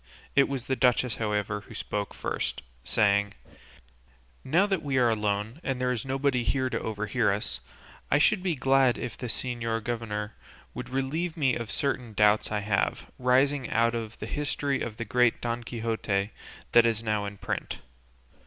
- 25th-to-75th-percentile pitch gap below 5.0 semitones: Yes, average, 3.9 semitones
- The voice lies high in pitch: No, low, 120 Hz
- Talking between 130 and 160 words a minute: No, average, 175 wpm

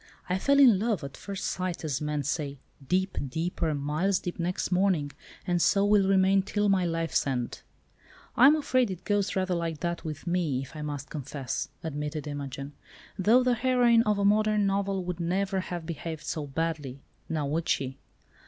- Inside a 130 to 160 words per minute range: No, average, 175 wpm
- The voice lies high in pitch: No, medium, 175 Hz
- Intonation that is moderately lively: Yes, average, 4.9 semitones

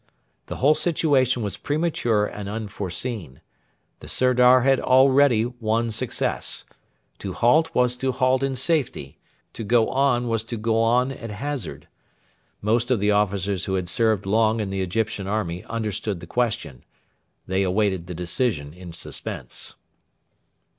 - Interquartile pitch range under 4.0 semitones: No, average, 4.3 semitones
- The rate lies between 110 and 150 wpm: Yes, average, 145 wpm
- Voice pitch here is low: Yes, low, 115 Hz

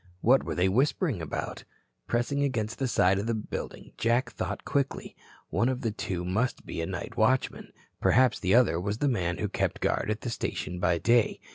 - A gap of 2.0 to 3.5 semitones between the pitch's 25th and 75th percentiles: No, average, 5.2 semitones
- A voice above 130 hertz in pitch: No, low, 115 Hz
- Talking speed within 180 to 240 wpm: Yes, average, 195 wpm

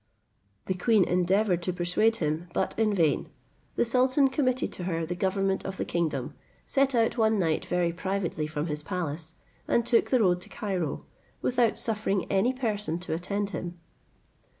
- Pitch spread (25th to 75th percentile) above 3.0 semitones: Yes, average, 4.6 semitones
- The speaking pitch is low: No, high, 190 Hz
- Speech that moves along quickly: No, average, 170 wpm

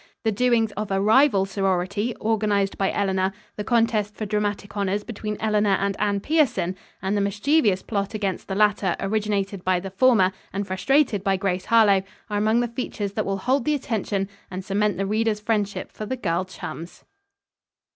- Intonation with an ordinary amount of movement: No, narrow, 2.1 semitones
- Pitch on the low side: No, high, 205 Hz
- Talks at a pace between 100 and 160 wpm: No, average, 175 wpm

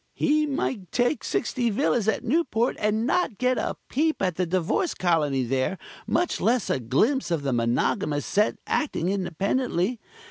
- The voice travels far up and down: Yes, wide, 7.4 semitones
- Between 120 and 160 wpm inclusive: Yes, average, 155 wpm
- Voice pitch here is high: Yes, high, 210 Hz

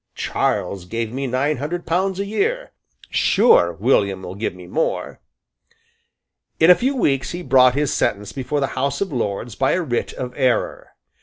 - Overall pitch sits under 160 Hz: Yes, low, 135 Hz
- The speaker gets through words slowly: No, average, 170 wpm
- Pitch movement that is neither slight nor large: No, wide, 7.2 semitones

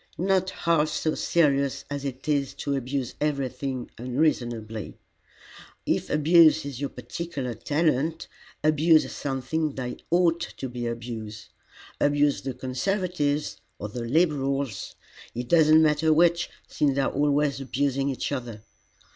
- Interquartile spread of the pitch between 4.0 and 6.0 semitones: No, average, 3.6 semitones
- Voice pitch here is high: No, medium, 140 Hz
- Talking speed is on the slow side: Yes, slow, 130 wpm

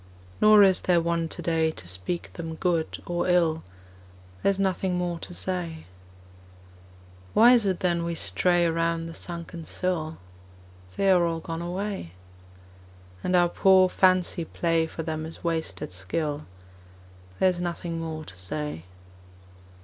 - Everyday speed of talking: Yes, average, 145 wpm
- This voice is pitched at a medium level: Yes, medium, 170 Hz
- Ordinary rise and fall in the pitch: No, narrow, 2.0 semitones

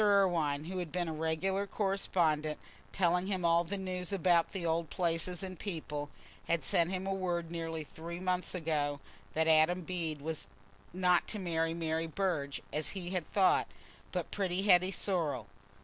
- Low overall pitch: No, medium, 170 Hz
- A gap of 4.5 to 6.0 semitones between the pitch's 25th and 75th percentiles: No, narrow, 2.5 semitones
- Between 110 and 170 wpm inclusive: Yes, average, 165 wpm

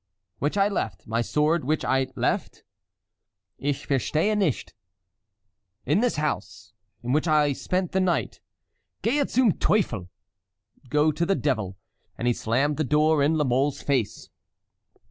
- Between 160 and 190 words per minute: No, average, 140 wpm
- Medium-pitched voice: Yes, medium, 150 Hz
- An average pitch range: Yes, average, 4.5 semitones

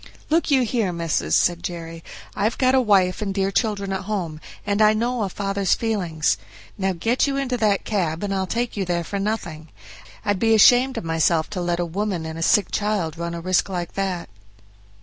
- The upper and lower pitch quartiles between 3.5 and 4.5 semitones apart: Yes, average, 4.0 semitones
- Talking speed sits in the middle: No, fast, 210 wpm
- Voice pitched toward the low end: No, high, 195 Hz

